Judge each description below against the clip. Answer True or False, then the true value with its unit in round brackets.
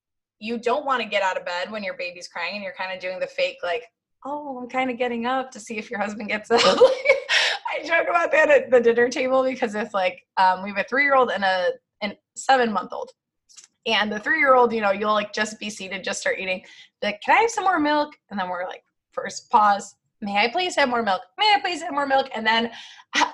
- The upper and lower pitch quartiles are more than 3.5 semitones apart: True (5.2 semitones)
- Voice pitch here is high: True (240 Hz)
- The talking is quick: True (255 wpm)